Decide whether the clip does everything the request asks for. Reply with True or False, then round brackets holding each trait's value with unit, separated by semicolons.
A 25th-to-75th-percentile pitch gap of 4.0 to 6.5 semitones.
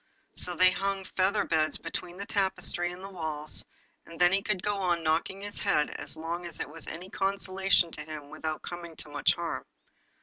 False (3.2 semitones)